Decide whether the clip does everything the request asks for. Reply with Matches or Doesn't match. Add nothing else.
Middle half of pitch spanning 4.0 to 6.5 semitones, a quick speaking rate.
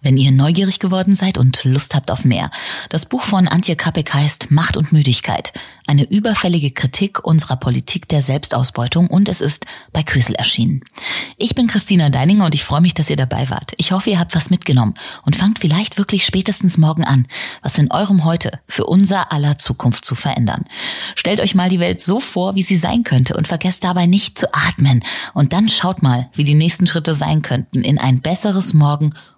Matches